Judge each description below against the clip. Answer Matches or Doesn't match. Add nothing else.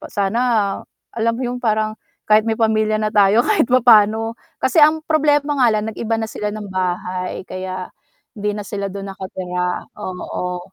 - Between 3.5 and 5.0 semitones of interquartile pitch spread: Doesn't match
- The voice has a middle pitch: Doesn't match